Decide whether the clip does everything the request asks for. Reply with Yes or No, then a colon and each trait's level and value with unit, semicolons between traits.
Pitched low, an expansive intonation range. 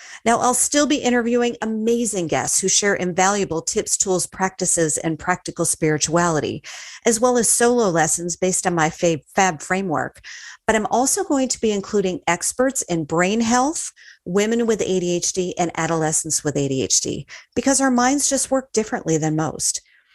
No: high, 190 Hz; wide, 6.2 semitones